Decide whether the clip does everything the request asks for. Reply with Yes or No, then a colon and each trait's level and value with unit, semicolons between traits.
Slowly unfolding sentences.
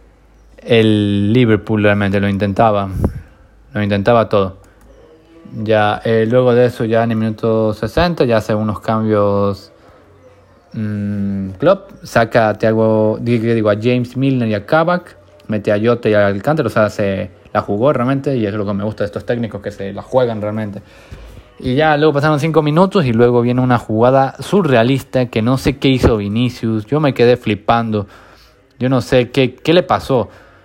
No: average, 175 wpm